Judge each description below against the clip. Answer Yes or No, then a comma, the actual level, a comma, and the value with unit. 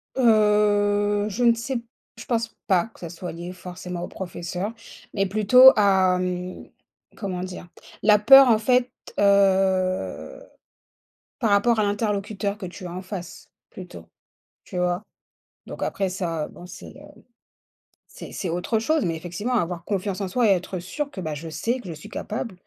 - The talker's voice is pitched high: Yes, high, 195 Hz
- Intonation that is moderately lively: Yes, average, 3.2 semitones